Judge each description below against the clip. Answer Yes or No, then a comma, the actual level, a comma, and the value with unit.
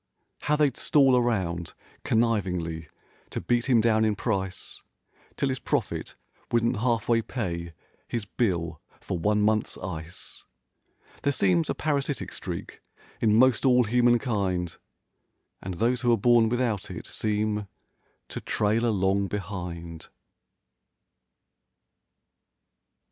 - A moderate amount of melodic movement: Yes, average, 4.5 semitones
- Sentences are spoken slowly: Yes, slow, 115 wpm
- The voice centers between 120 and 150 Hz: No, low, 110 Hz